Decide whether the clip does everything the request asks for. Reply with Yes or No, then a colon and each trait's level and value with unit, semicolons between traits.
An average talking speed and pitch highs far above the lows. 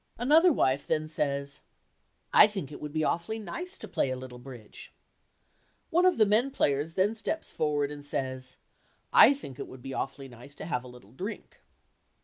Yes: average, 185 wpm; wide, 8.5 semitones